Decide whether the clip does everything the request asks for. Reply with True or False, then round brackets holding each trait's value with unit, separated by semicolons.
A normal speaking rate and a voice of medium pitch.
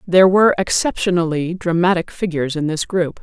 True (150 wpm; 175 Hz)